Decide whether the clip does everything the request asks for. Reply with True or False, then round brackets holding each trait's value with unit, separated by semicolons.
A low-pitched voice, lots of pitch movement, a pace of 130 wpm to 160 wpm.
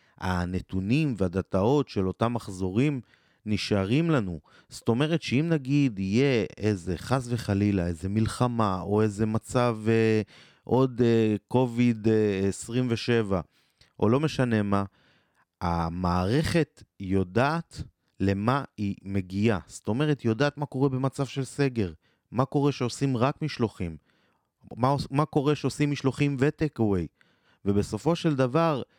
False (115 Hz; 5.8 semitones; 120 wpm)